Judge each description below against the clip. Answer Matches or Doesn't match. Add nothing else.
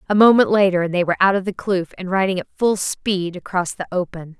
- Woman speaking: Matches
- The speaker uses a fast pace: Matches